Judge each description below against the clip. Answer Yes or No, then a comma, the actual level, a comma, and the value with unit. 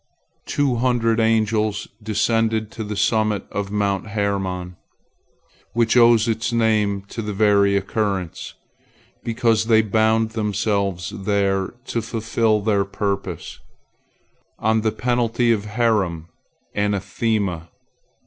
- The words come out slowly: Yes, slow, 110 wpm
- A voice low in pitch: Yes, low, 110 Hz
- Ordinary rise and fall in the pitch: No, narrow, 2.2 semitones